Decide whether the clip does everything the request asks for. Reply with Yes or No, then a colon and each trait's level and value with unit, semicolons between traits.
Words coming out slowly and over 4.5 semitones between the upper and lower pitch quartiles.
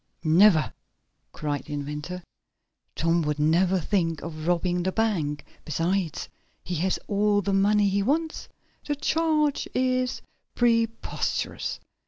Yes: slow, 120 wpm; wide, 5.6 semitones